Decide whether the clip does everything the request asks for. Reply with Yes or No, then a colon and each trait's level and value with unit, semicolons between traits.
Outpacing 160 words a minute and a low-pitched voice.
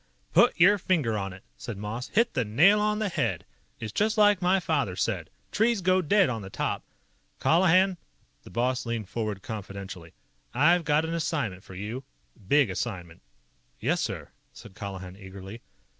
Yes: average, 170 wpm; low, 120 Hz